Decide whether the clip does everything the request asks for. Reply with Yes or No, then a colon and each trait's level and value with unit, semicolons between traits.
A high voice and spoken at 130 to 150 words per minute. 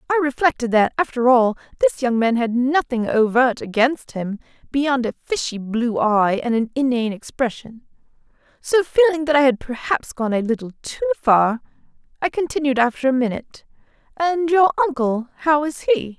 No: very high, 265 Hz; average, 165 wpm